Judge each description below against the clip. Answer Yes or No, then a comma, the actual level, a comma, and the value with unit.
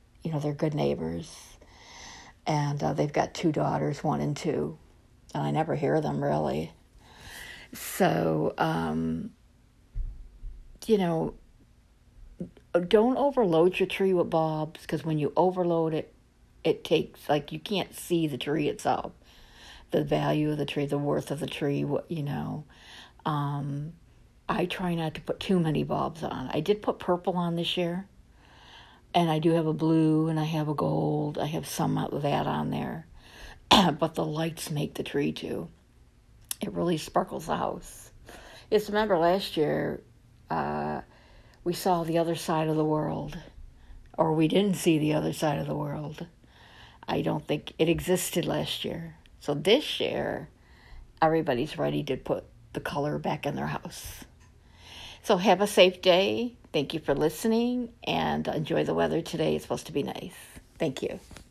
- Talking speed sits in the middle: Yes, average, 165 wpm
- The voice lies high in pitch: No, medium, 155 Hz